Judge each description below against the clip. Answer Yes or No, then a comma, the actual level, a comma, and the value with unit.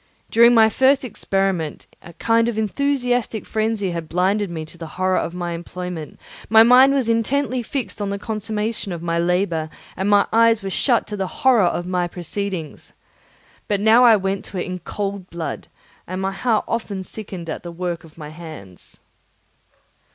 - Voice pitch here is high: Yes, high, 195 Hz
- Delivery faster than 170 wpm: Yes, average, 180 wpm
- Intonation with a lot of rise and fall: No, average, 4.5 semitones